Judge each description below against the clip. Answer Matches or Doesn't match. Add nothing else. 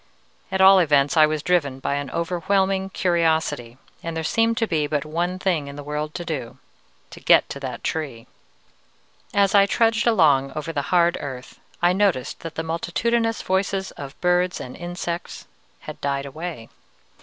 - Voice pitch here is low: Doesn't match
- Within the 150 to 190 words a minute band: Matches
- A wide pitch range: Doesn't match